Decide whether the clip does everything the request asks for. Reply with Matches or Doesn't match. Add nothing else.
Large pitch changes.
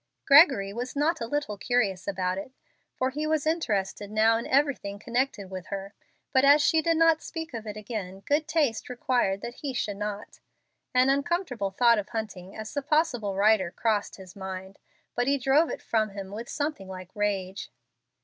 Matches